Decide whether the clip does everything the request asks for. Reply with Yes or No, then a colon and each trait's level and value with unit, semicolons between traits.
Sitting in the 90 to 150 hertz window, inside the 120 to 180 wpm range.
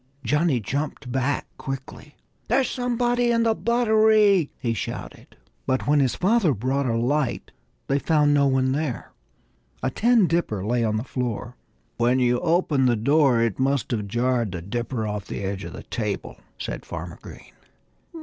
Yes: low, 135 Hz; average, 165 wpm